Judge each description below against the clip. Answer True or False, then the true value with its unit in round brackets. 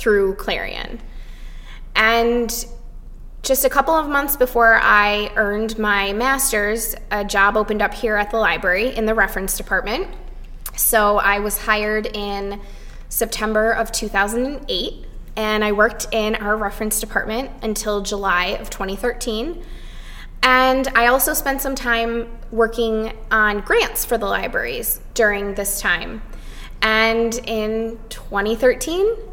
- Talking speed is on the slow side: True (125 wpm)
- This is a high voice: True (220 Hz)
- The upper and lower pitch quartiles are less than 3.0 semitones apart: True (2.5 semitones)